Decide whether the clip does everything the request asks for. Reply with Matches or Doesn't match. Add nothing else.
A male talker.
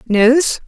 Doesn't match